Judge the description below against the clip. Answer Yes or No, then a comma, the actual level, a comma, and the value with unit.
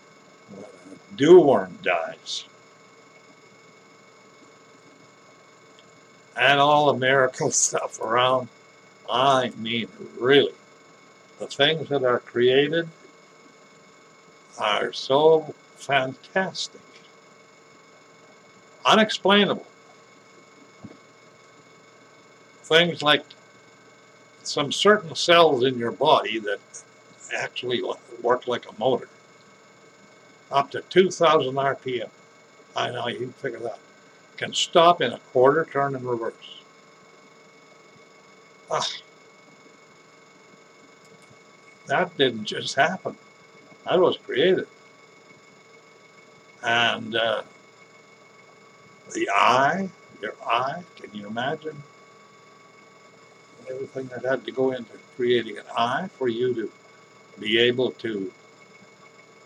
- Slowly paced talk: Yes, slow, 85 wpm